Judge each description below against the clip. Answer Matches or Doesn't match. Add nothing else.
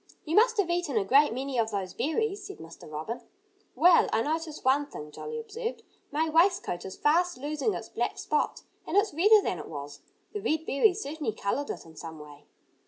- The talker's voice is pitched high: Matches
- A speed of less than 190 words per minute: Doesn't match